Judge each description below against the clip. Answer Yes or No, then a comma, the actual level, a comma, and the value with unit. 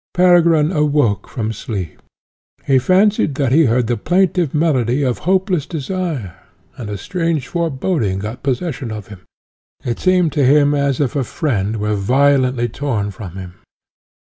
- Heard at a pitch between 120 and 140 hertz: Yes, low, 135 Hz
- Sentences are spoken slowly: No, average, 150 wpm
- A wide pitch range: Yes, wide, 6.4 semitones